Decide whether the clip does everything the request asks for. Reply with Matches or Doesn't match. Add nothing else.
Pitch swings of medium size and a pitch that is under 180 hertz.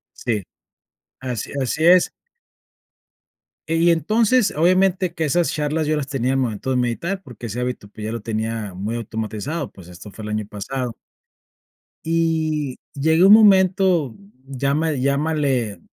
Doesn't match